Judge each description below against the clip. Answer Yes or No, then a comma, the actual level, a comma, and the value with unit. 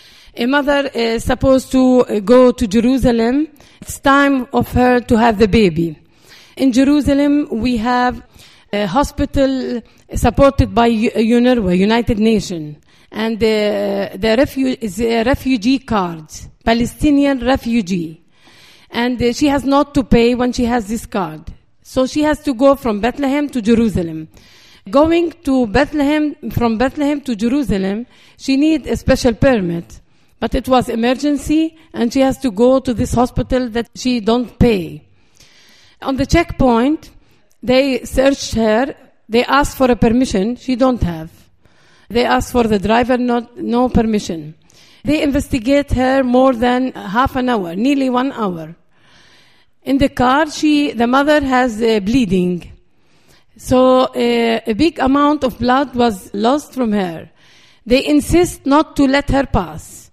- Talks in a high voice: Yes, very high, 250 Hz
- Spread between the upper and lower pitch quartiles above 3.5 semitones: No, average, 3.1 semitones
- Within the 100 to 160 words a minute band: Yes, average, 150 wpm